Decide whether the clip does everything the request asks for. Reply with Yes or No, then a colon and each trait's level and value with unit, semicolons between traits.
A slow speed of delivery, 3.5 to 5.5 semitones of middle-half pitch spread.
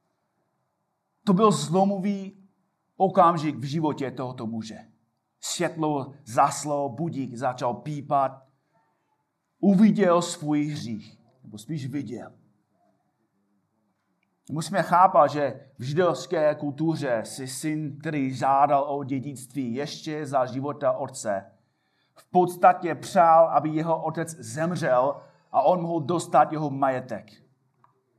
Yes: slow, 100 wpm; average, 3.9 semitones